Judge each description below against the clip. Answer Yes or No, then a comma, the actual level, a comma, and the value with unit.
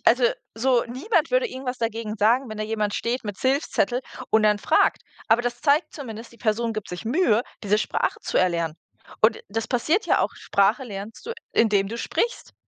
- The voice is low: No, high, 230 Hz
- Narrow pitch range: No, average, 3.5 semitones